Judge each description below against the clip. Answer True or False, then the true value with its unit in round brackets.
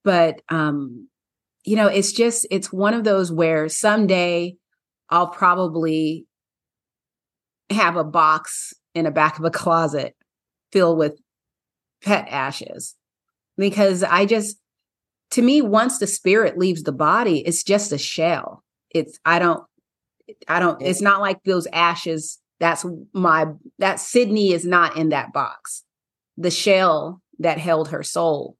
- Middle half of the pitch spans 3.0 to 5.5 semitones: True (3.7 semitones)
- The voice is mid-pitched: True (175 Hz)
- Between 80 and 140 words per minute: True (135 wpm)